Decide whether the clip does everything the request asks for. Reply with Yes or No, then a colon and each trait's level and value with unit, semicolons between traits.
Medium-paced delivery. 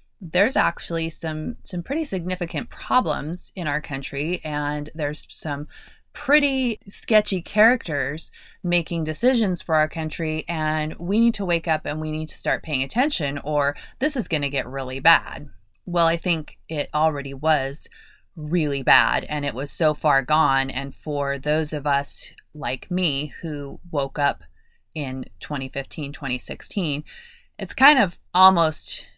Yes: average, 150 wpm